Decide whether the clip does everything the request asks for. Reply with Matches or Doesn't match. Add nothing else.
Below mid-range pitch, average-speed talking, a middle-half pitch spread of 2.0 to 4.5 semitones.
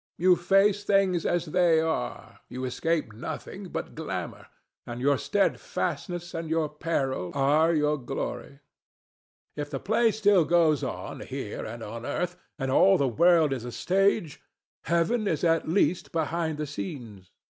Doesn't match